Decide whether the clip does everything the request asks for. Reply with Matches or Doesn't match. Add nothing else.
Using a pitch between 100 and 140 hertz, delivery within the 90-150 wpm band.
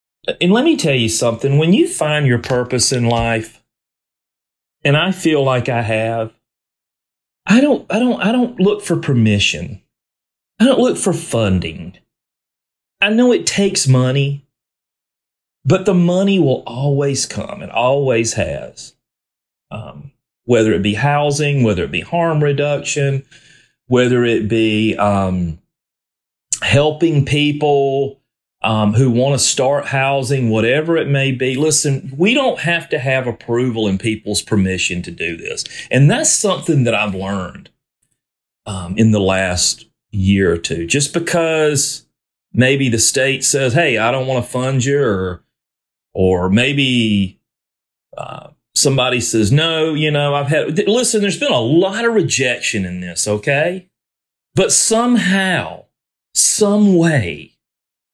Matches